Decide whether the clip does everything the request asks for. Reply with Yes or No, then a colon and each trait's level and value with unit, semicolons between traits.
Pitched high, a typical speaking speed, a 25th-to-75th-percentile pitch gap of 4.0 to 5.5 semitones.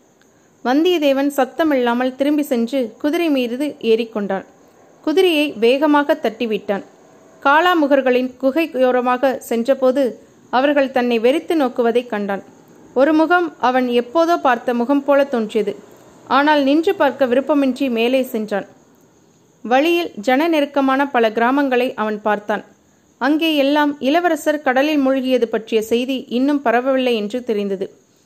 No: very high, 260 Hz; average, 110 wpm; average, 3.5 semitones